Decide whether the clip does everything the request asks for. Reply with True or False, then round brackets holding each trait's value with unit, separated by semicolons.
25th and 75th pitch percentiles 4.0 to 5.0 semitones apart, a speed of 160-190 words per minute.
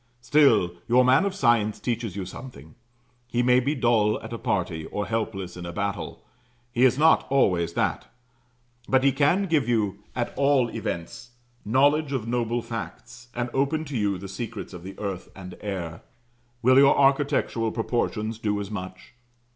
True (4.6 semitones; 170 wpm)